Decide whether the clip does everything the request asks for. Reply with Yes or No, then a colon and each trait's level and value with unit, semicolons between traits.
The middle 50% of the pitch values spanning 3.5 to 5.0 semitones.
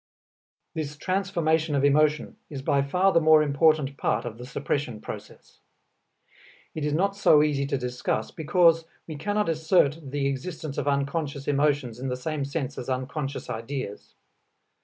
No: narrow, 2.5 semitones